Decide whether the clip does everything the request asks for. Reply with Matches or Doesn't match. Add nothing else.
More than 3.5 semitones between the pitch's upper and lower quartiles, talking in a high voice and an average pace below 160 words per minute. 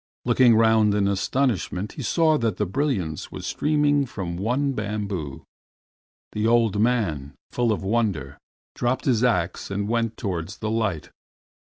Doesn't match